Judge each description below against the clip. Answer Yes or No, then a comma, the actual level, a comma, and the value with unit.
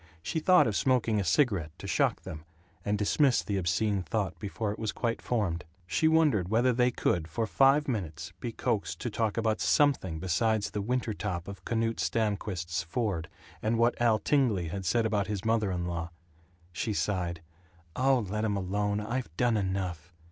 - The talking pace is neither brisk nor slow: Yes, average, 180 wpm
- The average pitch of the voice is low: Yes, low, 105 Hz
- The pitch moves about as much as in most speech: Yes, average, 4.2 semitones